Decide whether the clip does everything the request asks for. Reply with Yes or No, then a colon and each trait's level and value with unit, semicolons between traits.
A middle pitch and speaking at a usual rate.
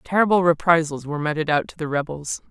Yes: medium, 160 Hz; average, 190 wpm